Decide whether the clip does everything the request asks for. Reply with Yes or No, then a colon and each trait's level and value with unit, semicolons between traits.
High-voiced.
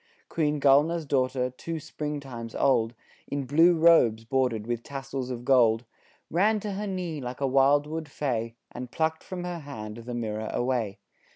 No: low, 135 Hz